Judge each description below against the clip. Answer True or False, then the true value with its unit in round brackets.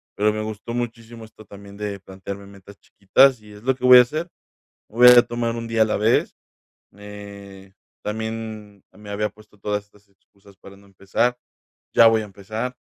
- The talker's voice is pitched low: True (105 Hz)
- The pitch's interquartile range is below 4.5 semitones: True (2.4 semitones)